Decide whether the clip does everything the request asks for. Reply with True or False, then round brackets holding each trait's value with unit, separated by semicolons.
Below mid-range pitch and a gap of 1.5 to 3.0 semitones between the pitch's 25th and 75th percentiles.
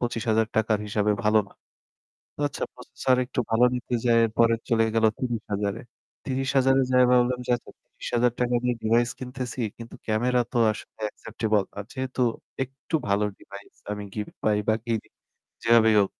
True (115 Hz; 2.5 semitones)